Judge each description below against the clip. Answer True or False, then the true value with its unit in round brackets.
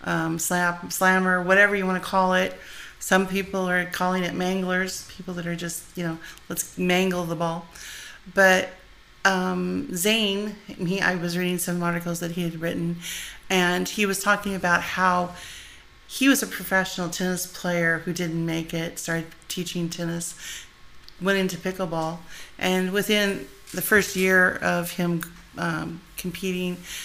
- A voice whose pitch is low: False (180 Hz)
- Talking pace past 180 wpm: False (155 wpm)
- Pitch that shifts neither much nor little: False (1.5 semitones)